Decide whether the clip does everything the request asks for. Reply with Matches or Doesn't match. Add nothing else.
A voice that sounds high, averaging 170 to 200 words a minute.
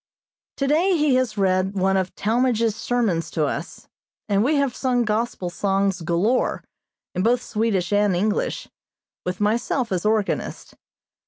Doesn't match